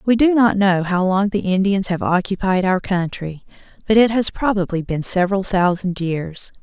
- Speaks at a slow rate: No, average, 180 wpm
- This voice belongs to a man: No, female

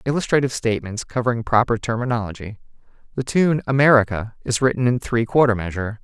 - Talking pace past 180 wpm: No, average, 140 wpm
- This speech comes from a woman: No, male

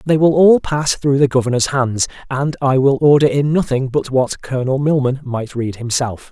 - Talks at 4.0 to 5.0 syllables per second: Yes, 4.9 syllables/s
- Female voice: No, male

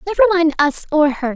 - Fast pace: Yes, fast, 220 wpm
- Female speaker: Yes, female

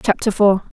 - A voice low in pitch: No, high, 205 Hz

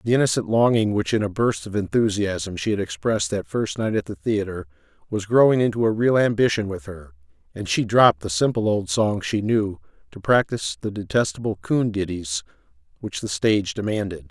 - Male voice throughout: Yes, male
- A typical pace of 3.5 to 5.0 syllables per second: No, 5.5 syllables/s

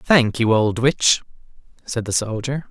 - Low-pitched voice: Yes, low, 120 Hz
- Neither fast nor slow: Yes, average, 155 wpm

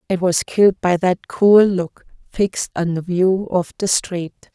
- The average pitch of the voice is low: No, medium, 185 Hz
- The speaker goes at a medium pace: Yes, average, 185 wpm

